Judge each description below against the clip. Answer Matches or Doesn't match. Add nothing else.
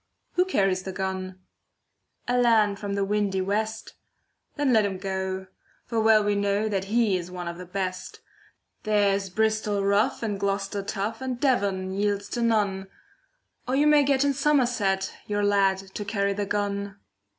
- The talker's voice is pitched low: Doesn't match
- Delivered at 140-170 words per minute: Matches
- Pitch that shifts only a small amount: Matches